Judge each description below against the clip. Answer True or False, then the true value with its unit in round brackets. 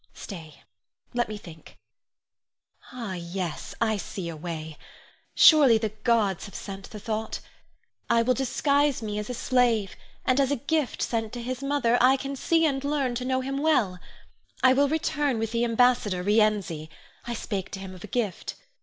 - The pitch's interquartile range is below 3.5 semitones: False (4.9 semitones)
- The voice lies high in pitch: True (230 Hz)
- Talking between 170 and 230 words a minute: True (175 wpm)